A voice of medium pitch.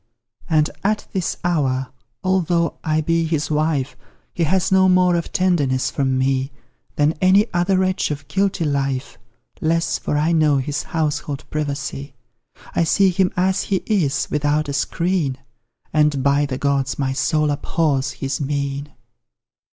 Yes: medium, 150 Hz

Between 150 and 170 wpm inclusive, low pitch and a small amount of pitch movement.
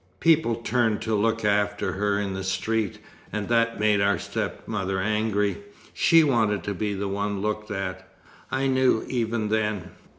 Yes: average, 160 wpm; low, 105 Hz; narrow, 1.9 semitones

